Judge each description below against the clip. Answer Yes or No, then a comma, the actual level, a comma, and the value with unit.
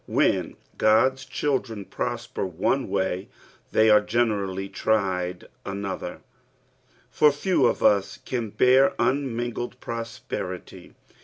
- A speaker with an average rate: No, slow, 105 wpm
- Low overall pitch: Yes, low, 115 Hz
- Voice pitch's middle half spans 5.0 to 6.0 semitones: No, average, 4.4 semitones